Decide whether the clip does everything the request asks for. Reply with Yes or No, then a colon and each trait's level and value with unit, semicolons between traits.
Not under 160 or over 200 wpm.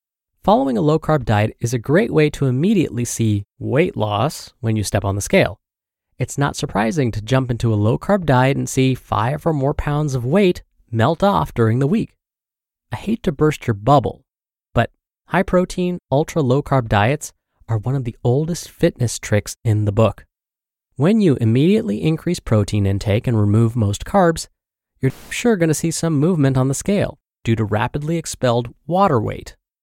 Yes: average, 185 wpm